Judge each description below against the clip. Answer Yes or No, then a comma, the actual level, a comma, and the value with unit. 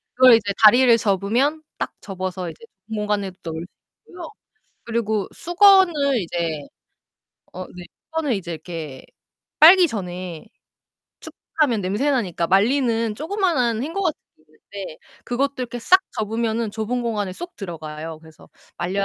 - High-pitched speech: Yes, high, 220 Hz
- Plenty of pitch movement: Yes, wide, 6.4 semitones